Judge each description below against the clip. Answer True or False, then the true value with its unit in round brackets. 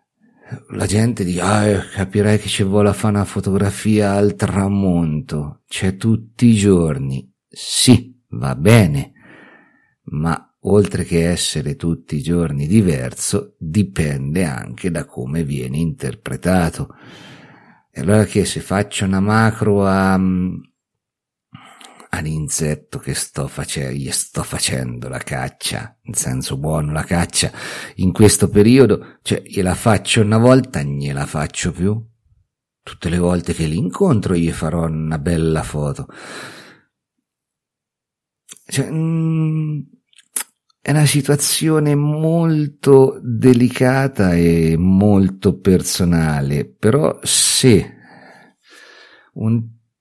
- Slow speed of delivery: True (110 wpm)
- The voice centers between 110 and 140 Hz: False (95 Hz)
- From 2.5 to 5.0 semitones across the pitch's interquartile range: False (5.5 semitones)